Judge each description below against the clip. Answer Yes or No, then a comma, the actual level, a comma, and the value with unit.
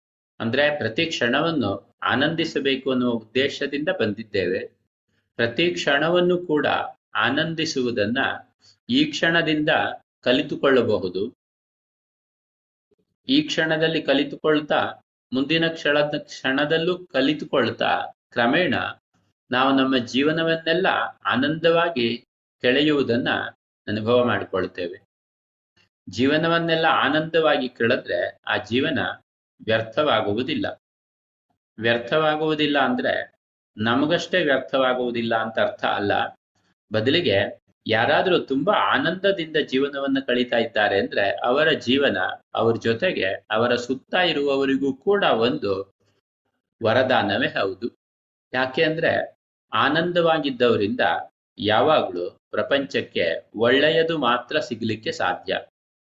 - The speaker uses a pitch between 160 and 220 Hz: No, medium, 140 Hz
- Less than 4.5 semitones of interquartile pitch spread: No, average, 5.2 semitones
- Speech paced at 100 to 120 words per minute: No, average, 75 wpm